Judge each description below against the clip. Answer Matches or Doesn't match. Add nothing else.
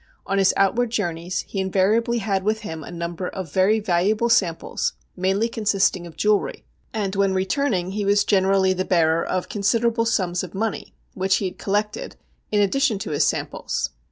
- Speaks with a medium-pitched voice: Doesn't match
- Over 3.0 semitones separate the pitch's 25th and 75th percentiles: Doesn't match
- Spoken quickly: Doesn't match